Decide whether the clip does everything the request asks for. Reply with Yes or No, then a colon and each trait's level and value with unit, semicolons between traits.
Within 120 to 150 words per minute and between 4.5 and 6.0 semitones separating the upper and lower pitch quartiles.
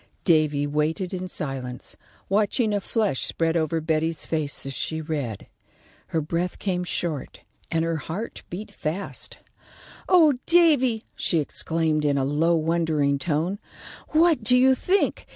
Yes: average, 140 wpm; average, 5.1 semitones